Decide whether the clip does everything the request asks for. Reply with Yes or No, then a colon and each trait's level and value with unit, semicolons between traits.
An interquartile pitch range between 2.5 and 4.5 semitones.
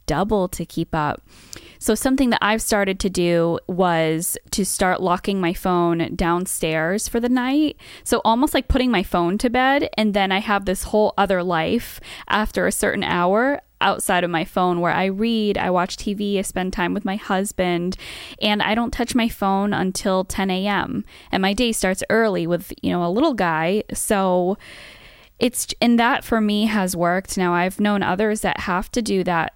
Yes: average, 3.8 semitones